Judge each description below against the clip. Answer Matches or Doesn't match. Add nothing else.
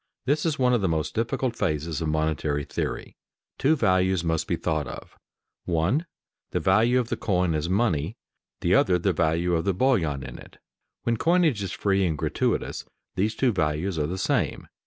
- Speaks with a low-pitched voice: Matches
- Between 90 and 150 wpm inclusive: Doesn't match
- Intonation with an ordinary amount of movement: Doesn't match